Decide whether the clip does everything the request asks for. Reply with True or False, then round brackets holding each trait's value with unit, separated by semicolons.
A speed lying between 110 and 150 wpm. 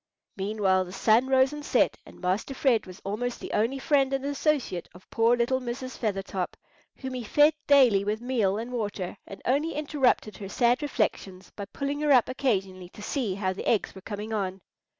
False (190 wpm)